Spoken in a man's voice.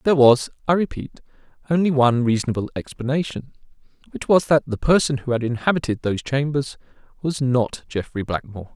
Yes: male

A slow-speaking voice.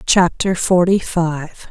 Yes: slow, 105 wpm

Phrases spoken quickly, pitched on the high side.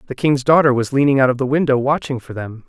No: fast, 270 wpm; low, 135 Hz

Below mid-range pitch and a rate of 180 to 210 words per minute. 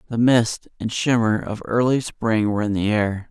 Yes: low, 110 Hz; average, 200 wpm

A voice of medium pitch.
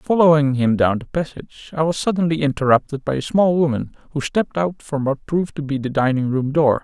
Yes: medium, 145 Hz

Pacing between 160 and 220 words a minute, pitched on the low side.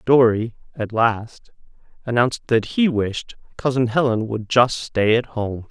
No: average, 145 wpm; low, 120 Hz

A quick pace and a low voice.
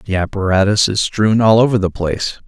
No: average, 195 wpm; low, 100 Hz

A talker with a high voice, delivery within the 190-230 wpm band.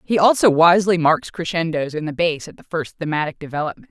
No: medium, 165 Hz; average, 200 wpm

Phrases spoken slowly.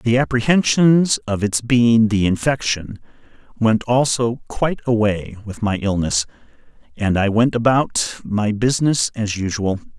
Yes: slow, 130 wpm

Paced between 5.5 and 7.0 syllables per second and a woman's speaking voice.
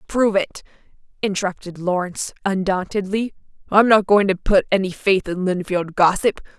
No: 5.2 syllables/s; female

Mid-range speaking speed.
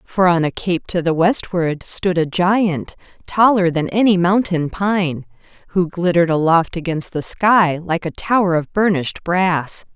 Yes: average, 165 wpm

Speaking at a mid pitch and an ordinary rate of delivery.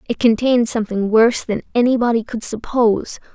No: high, 230 Hz; average, 145 wpm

